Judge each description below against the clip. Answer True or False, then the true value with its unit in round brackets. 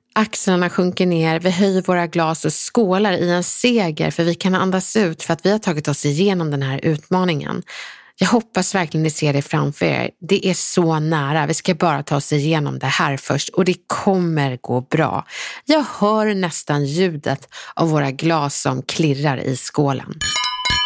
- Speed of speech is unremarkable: True (185 wpm)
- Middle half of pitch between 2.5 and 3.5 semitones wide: False (4.1 semitones)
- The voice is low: False (170 Hz)